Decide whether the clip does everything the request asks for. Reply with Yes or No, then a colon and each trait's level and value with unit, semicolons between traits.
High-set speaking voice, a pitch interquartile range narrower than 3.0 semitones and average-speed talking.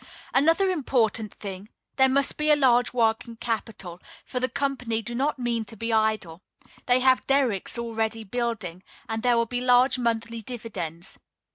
Yes: high, 235 Hz; narrow, 2.5 semitones; average, 160 wpm